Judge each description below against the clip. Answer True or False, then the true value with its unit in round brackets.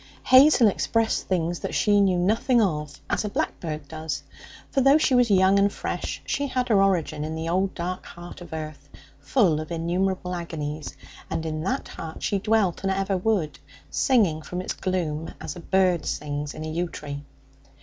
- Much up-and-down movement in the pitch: False (4.3 semitones)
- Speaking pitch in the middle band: True (180 Hz)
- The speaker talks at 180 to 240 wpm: True (185 wpm)